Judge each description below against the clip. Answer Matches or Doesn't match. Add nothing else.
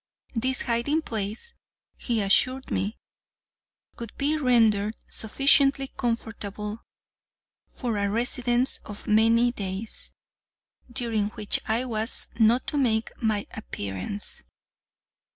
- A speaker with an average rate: Doesn't match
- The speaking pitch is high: Matches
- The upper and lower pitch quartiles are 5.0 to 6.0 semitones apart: Doesn't match